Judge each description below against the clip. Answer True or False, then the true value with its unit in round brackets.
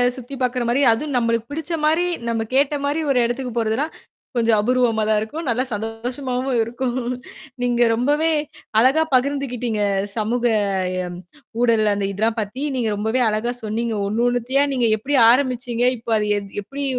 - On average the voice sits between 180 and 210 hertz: False (245 Hz)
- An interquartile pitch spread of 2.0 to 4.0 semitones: True (3.0 semitones)